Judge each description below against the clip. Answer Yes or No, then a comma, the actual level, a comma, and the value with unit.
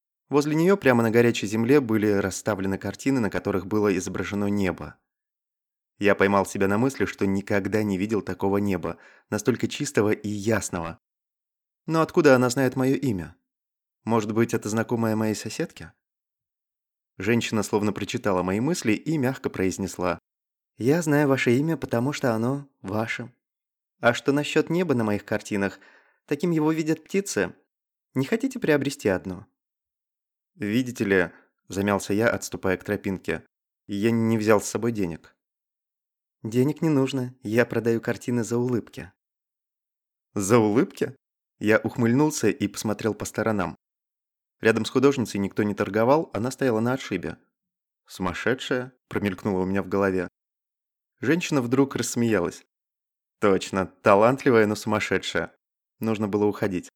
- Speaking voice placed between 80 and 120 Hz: Yes, low, 110 Hz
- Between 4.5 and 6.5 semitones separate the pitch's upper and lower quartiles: Yes, average, 4.8 semitones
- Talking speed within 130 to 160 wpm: Yes, average, 135 wpm